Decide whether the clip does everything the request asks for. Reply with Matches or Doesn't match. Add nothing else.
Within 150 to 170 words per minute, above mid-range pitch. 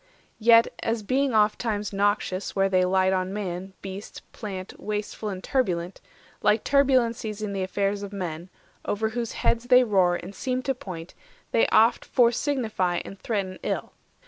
Matches